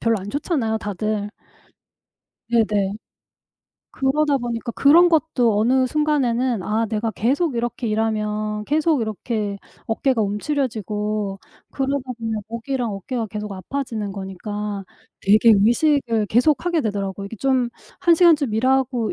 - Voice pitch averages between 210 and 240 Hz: Yes, high, 230 Hz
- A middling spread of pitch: Yes, average, 4.2 semitones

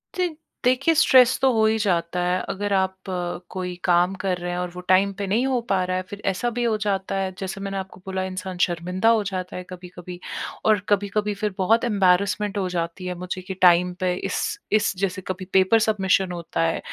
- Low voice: No, high, 190 Hz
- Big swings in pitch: No, narrow, 2.4 semitones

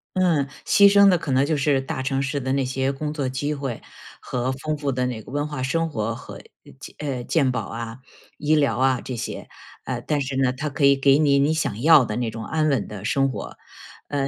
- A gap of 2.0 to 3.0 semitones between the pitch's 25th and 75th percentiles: Yes, narrow, 2.6 semitones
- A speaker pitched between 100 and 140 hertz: Yes, low, 135 Hz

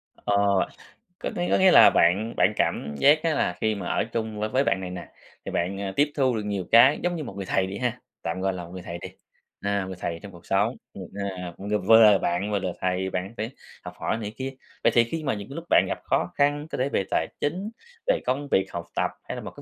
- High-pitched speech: No, low, 105 Hz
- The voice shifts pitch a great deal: Yes, wide, 5.9 semitones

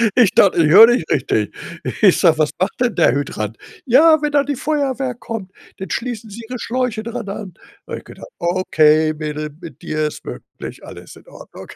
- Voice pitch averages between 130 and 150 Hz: No, high, 195 Hz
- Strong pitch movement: Yes, wide, 8.1 semitones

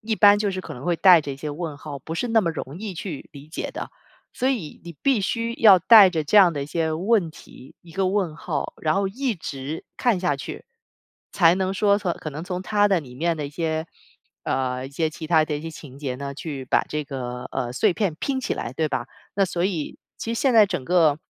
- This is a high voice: No, medium, 165 Hz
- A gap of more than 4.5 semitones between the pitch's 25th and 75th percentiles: Yes, average, 5.1 semitones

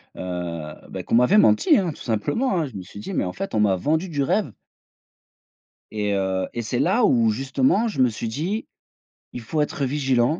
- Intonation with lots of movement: Yes, wide, 7.2 semitones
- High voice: No, low, 125 Hz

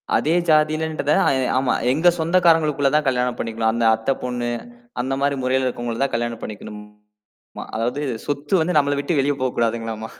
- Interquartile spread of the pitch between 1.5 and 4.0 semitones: No, average, 4.4 semitones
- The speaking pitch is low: Yes, low, 130 Hz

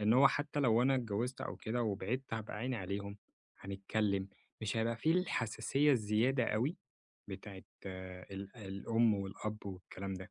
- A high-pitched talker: No, low, 110 Hz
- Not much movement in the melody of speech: No, average, 3.9 semitones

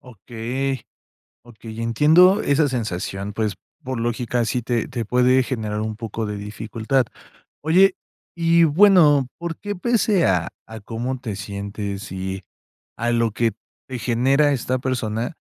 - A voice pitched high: No, low, 120 Hz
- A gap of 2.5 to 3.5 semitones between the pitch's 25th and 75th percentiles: No, average, 4.1 semitones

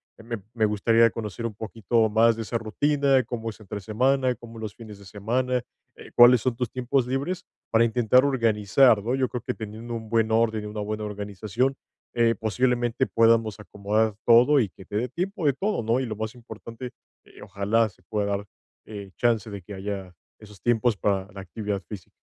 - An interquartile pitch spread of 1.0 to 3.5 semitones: Yes, average, 2.7 semitones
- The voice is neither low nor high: No, low, 115 Hz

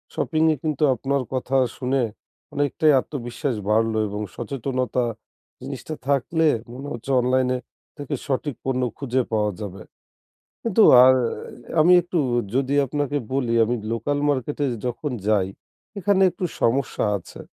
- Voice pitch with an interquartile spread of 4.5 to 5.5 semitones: No, average, 3.1 semitones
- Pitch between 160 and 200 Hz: No, low, 135 Hz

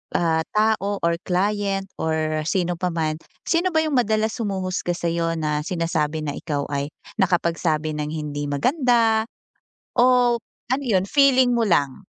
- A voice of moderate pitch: Yes, medium, 180 Hz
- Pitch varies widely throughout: Yes, wide, 5.8 semitones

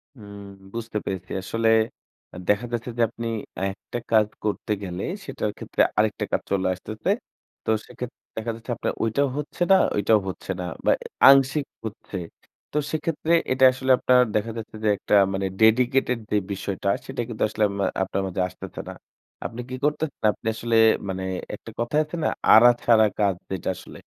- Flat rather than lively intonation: No, average, 3.8 semitones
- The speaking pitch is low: Yes, low, 110 Hz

